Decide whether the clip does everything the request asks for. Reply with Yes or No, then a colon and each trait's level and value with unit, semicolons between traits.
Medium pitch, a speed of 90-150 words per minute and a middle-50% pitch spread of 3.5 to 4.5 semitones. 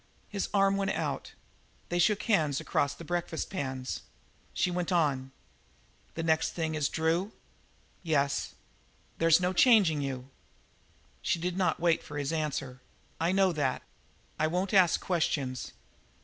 Yes: medium, 165 Hz; average, 140 wpm; average, 4.1 semitones